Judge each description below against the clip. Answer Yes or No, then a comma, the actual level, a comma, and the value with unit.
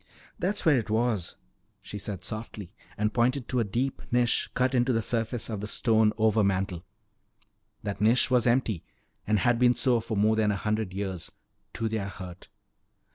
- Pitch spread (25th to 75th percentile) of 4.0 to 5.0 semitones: No, average, 2.9 semitones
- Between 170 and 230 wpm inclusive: Yes, average, 175 wpm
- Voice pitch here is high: No, low, 110 Hz